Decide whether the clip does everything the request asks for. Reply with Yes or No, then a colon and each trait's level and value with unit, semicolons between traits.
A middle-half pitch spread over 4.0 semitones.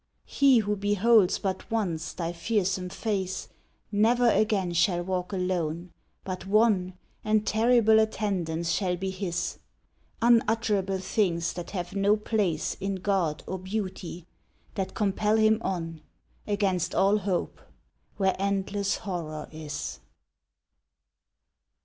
No: average, 2.9 semitones